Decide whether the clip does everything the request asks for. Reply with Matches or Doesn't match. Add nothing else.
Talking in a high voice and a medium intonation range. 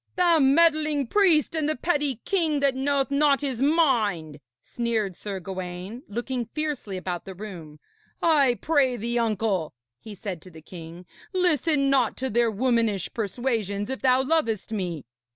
Doesn't match